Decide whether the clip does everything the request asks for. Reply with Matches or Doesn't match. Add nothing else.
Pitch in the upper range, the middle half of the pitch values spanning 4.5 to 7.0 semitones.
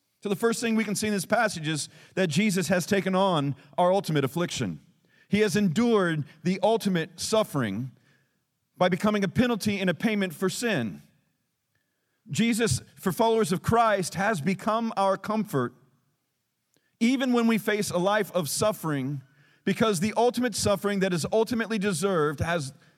Matches